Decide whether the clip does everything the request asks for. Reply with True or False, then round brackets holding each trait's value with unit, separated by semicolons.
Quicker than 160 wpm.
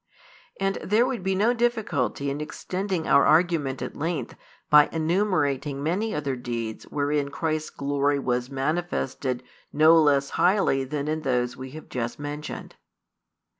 False (140 wpm)